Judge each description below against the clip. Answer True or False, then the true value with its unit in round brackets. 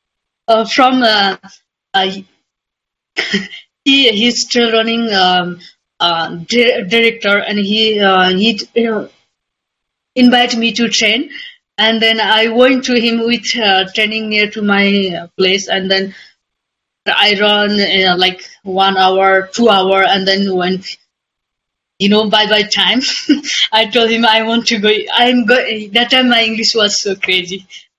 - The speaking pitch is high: True (215 Hz)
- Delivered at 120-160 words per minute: True (150 wpm)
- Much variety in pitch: False (3.3 semitones)